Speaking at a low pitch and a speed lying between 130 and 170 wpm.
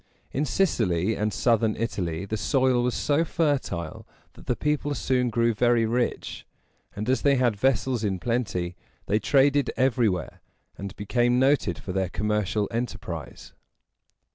Yes: low, 115 Hz; average, 140 wpm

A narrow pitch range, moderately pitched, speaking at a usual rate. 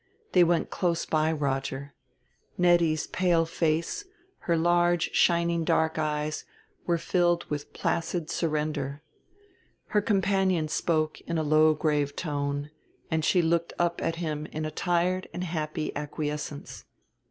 No: narrow, 2.3 semitones; medium, 160 Hz; slow, 130 wpm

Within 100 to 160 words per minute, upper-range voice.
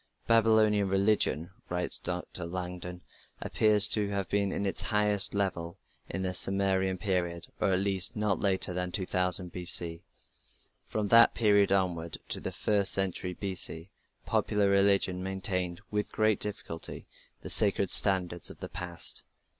No: average, 140 wpm; very low, 95 Hz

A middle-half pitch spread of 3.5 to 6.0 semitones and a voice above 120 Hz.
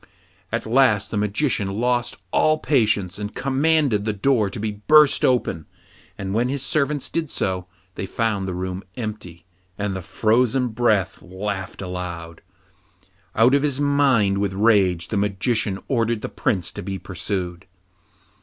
No: average, 4.7 semitones; low, 105 Hz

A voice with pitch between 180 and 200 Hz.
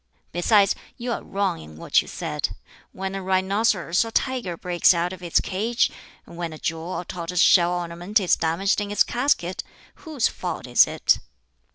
Yes: medium, 185 Hz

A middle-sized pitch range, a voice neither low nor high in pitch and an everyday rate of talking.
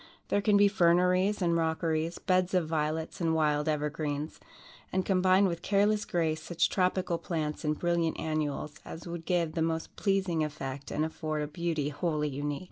Yes: average, 3.0 semitones; medium, 165 Hz; average, 170 wpm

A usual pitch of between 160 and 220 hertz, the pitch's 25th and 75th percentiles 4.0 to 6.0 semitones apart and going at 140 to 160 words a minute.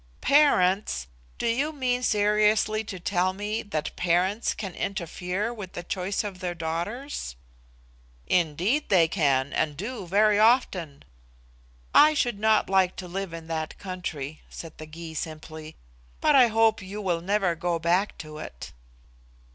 Yes: medium, 185 Hz; average, 4.3 semitones; average, 145 wpm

